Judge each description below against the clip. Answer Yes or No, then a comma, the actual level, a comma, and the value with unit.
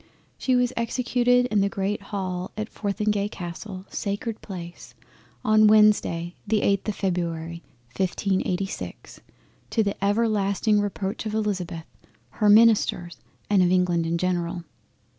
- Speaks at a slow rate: Yes, slow, 120 wpm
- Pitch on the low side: No, high, 200 Hz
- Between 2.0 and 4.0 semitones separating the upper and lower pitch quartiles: Yes, average, 3.0 semitones